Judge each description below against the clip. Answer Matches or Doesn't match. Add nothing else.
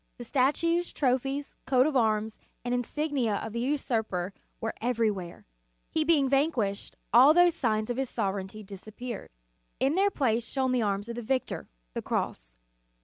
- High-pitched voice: Matches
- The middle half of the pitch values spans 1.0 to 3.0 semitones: Doesn't match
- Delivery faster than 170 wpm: Doesn't match